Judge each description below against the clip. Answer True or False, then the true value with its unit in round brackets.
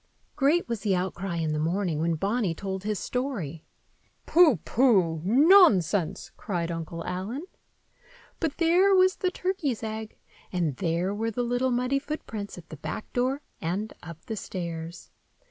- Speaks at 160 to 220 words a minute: False (150 wpm)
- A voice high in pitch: True (205 Hz)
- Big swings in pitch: True (7.3 semitones)